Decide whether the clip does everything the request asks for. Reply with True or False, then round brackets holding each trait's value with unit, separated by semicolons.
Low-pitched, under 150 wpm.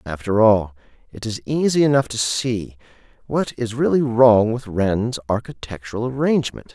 True (115 Hz; 140 wpm)